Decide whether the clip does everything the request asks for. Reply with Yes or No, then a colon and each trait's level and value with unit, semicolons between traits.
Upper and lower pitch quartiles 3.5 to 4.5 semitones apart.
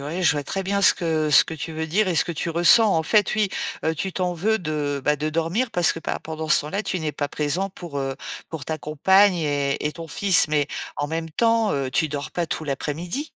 Yes: average, 3.9 semitones